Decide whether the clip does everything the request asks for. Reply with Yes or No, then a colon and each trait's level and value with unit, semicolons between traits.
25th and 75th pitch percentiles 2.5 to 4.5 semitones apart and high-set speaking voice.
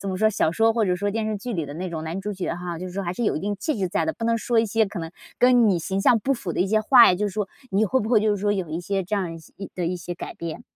Yes: average, 3.4 semitones; high, 200 Hz